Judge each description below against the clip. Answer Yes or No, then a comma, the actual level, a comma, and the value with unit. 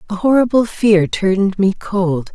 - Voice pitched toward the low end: No, high, 200 Hz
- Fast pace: No, average, 155 wpm